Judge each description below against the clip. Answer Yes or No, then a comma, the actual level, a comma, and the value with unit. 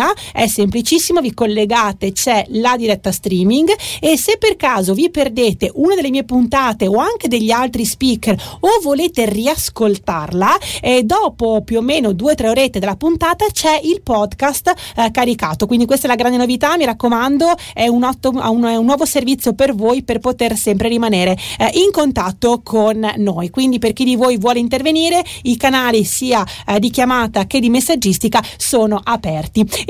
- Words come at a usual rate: No, fast, 175 wpm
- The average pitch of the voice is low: No, high, 240 Hz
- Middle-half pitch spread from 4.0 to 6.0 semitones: Yes, average, 4.4 semitones